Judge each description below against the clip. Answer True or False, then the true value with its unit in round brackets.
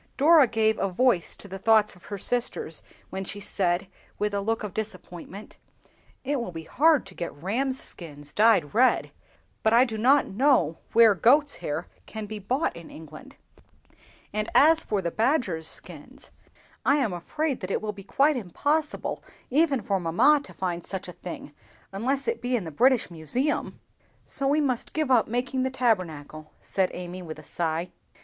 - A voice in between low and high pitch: False (215 Hz)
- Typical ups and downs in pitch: False (6.6 semitones)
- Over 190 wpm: False (180 wpm)